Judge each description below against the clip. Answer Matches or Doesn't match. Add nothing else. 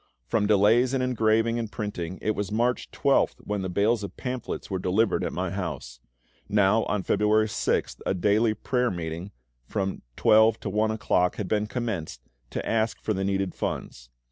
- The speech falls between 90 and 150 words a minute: Doesn't match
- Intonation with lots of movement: Doesn't match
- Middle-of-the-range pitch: Doesn't match